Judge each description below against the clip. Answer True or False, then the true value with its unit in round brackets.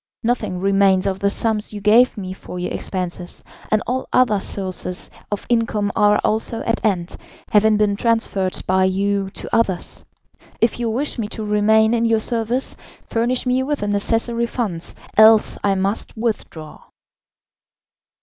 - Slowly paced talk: False (155 wpm)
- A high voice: True (210 Hz)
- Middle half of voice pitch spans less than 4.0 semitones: True (2.8 semitones)